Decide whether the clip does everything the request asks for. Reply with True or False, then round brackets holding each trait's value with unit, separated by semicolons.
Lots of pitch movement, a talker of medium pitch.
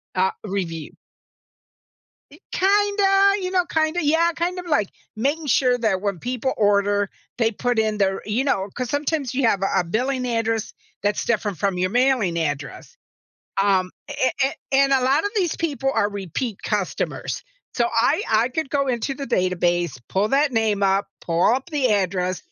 False (6.0 semitones; 230 Hz)